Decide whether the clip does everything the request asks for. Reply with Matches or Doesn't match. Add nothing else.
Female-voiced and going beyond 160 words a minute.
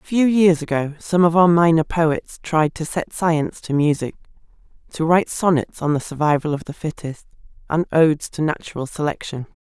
Matches